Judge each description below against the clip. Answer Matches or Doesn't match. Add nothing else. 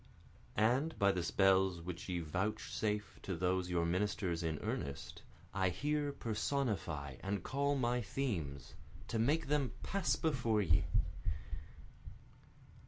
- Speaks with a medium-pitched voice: Doesn't match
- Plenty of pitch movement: Matches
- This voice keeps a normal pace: Doesn't match